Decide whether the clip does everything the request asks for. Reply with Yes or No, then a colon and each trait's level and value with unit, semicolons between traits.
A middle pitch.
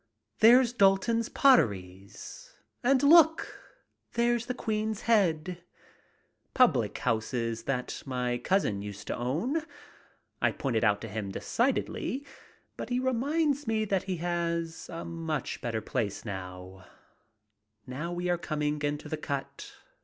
Yes: medium, 170 Hz